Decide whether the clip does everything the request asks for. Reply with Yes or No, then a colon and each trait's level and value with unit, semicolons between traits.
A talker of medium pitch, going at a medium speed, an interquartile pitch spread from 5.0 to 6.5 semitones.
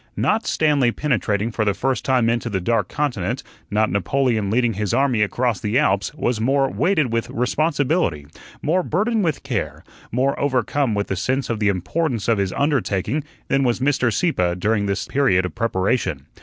No: low, 120 Hz; average, 175 wpm; wide, 5.4 semitones